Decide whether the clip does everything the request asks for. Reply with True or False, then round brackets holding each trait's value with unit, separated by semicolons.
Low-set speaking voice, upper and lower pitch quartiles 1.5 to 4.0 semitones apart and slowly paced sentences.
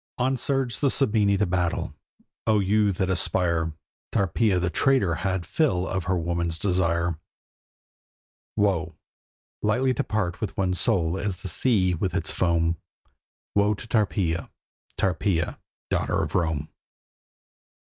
True (95 Hz; 3.7 semitones; 130 wpm)